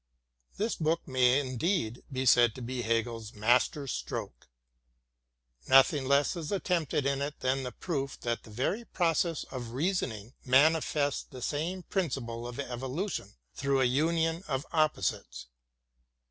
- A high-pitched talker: No, low, 135 Hz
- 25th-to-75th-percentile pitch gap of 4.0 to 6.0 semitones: Yes, average, 4.6 semitones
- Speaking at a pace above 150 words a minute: No, average, 145 wpm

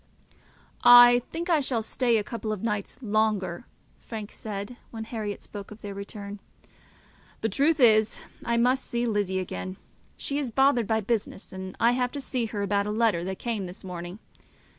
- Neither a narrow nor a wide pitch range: Yes, average, 3.2 semitones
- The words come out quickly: No, average, 180 wpm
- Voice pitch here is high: Yes, high, 220 Hz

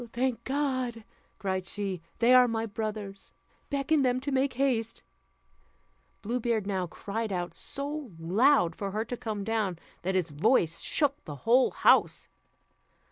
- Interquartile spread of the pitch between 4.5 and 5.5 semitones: Yes, average, 4.9 semitones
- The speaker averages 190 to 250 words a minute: No, average, 145 wpm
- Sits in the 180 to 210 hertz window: No, high, 225 Hz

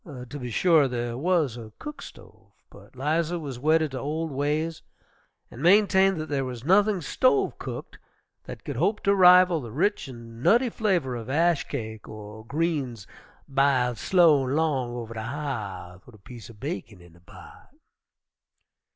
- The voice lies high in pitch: No, medium, 140 Hz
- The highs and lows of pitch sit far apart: Yes, wide, 6.0 semitones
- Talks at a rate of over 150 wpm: Yes, average, 165 wpm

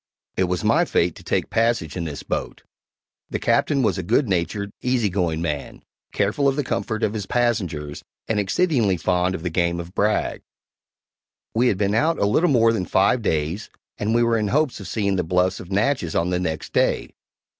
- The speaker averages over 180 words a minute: Yes, average, 200 wpm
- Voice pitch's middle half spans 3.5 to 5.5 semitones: Yes, average, 4.7 semitones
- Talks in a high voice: No, low, 100 Hz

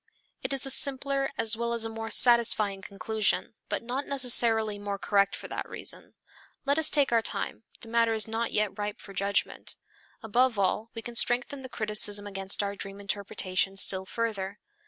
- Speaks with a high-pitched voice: Yes, high, 220 Hz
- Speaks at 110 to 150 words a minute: No, average, 180 wpm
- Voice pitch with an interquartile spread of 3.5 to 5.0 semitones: No, average, 2.9 semitones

